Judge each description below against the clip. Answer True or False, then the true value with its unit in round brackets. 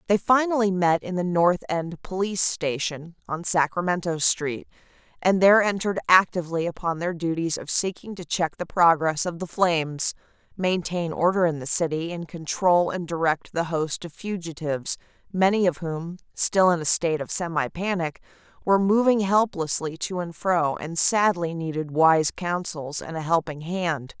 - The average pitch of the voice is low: False (170 Hz)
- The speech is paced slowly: False (165 wpm)